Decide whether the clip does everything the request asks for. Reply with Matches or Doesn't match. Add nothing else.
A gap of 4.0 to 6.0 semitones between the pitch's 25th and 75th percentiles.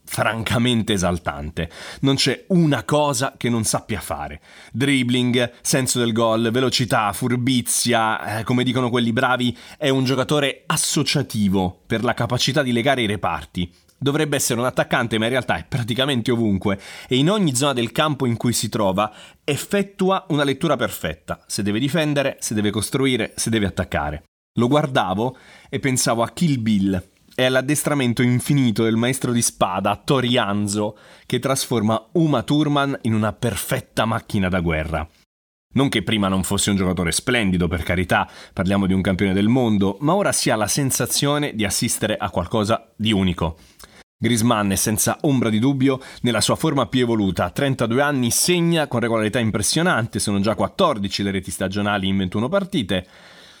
Matches